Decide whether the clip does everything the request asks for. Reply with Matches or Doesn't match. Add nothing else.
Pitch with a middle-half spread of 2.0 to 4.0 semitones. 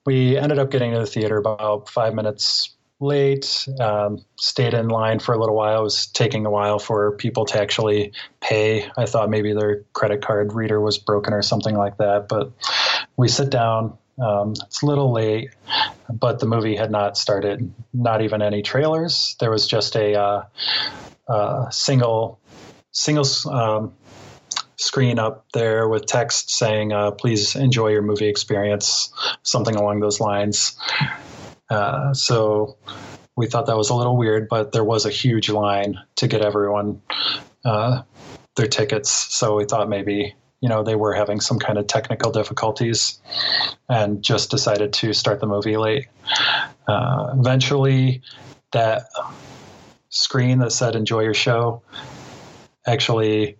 Matches